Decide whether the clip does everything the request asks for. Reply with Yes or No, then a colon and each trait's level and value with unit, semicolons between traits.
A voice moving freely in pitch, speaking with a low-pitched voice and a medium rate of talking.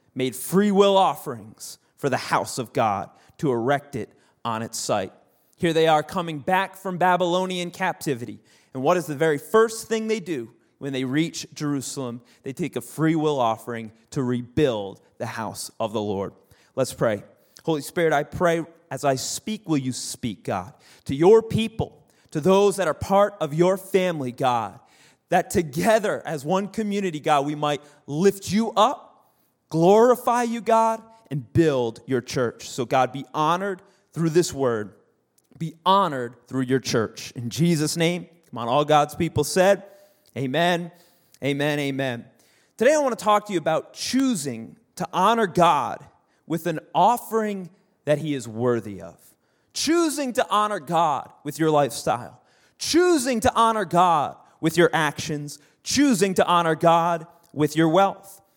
No: wide, 5.7 semitones; medium, 165 Hz; average, 160 wpm